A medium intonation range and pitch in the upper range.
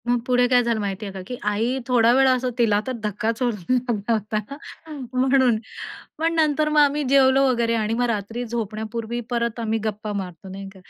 Yes: average, 3.1 semitones; high, 235 Hz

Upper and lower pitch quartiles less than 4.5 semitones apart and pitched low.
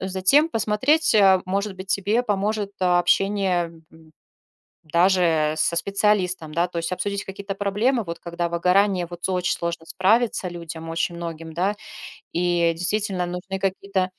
No: average, 2.8 semitones; medium, 185 Hz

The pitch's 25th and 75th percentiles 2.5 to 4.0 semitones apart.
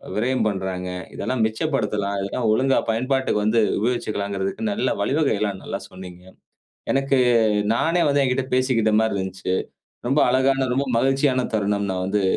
No: average, 5.0 semitones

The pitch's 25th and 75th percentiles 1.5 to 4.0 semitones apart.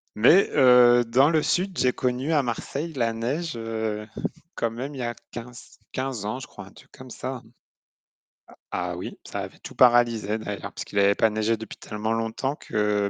Yes: average, 2.9 semitones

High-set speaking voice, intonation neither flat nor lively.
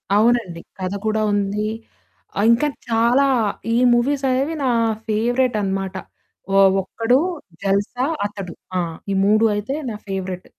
Yes: high, 215 Hz; average, 3.7 semitones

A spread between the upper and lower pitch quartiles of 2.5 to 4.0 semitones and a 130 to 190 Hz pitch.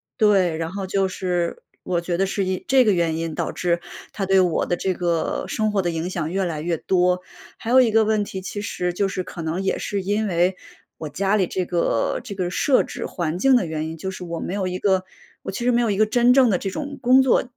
Yes: average, 3.2 semitones; medium, 185 Hz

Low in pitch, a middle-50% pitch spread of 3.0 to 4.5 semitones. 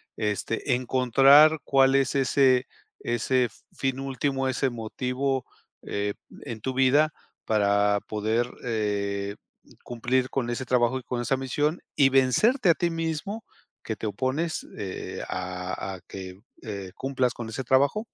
Yes: low, 125 Hz; average, 3.9 semitones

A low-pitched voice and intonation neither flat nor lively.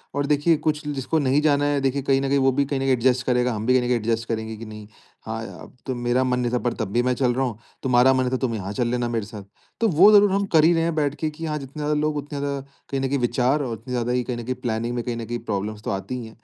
Yes: low, 130 Hz; average, 3.2 semitones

